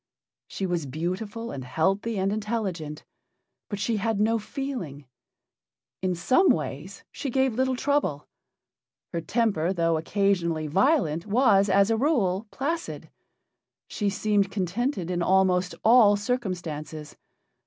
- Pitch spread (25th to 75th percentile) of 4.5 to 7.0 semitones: Yes, average, 5.1 semitones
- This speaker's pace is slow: Yes, slow, 120 wpm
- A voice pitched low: No, high, 195 Hz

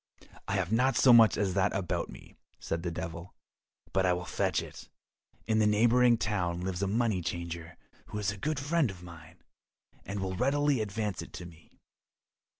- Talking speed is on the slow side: No, average, 185 wpm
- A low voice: Yes, low, 100 Hz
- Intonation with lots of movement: No, average, 4.5 semitones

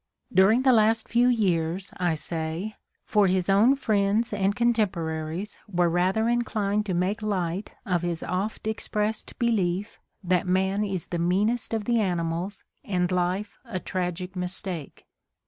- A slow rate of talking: No, average, 145 wpm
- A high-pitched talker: Yes, high, 195 Hz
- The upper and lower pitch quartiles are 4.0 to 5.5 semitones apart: No, average, 3.3 semitones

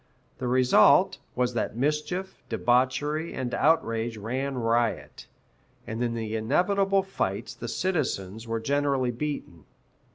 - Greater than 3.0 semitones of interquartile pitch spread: Yes, average, 4.7 semitones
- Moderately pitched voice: No, low, 125 Hz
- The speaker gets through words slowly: Yes, slow, 120 wpm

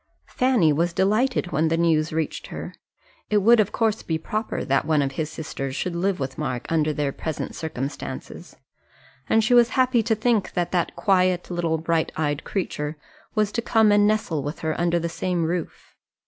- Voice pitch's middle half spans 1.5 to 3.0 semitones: No, average, 5.2 semitones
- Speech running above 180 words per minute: Yes, average, 190 wpm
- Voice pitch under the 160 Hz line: No, medium, 170 Hz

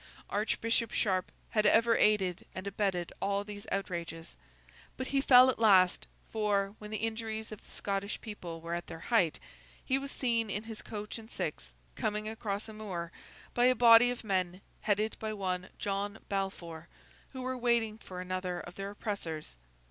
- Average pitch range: Yes, average, 3.3 semitones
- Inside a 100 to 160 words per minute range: No, average, 170 wpm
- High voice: Yes, high, 205 Hz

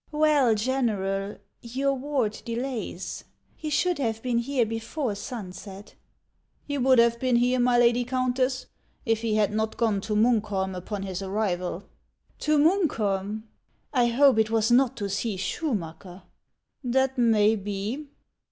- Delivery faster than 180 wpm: No, average, 155 wpm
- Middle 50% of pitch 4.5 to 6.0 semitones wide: No, average, 4.0 semitones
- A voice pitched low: No, high, 230 Hz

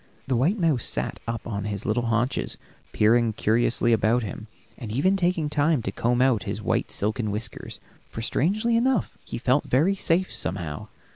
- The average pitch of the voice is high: No, low, 120 Hz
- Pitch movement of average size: No, wide, 6.5 semitones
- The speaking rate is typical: Yes, average, 170 wpm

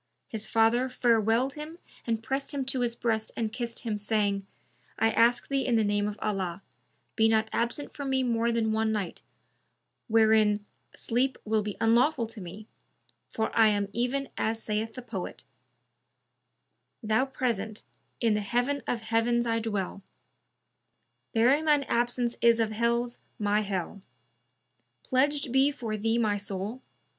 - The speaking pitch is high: Yes, high, 225 Hz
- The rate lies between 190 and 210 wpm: No, average, 155 wpm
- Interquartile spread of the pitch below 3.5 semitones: Yes, narrow, 2.4 semitones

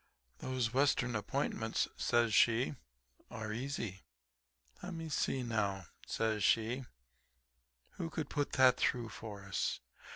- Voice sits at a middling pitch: No, low, 120 Hz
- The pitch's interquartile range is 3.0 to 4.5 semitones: Yes, average, 3.5 semitones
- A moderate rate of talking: No, slow, 110 wpm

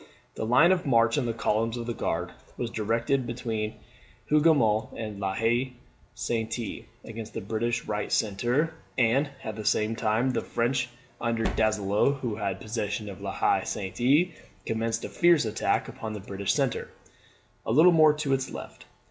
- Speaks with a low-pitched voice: Yes, low, 115 Hz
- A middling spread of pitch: Yes, average, 3.1 semitones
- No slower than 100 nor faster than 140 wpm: No, average, 165 wpm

